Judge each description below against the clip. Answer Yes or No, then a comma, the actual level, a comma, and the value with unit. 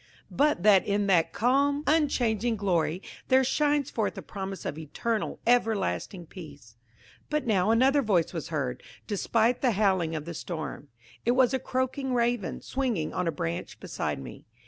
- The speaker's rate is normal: Yes, average, 160 wpm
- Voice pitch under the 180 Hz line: No, high, 215 Hz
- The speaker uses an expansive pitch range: Yes, wide, 6.8 semitones